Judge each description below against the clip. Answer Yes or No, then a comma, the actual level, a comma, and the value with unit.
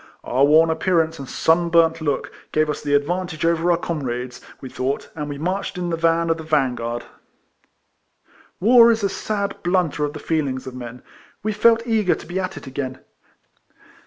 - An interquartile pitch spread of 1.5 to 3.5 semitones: No, average, 4.1 semitones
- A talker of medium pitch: Yes, medium, 160 Hz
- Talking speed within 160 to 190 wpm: Yes, average, 185 wpm